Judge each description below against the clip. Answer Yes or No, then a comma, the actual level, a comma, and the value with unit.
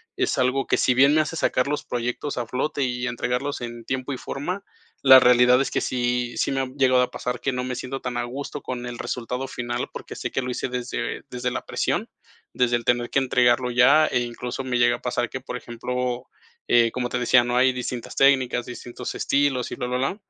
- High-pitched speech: No, low, 125 Hz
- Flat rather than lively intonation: Yes, narrow, 1.4 semitones